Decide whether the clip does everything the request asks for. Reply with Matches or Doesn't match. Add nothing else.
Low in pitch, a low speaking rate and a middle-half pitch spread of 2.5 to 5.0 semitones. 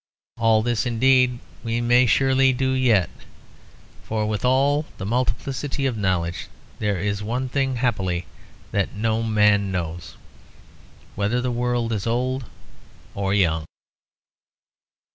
Matches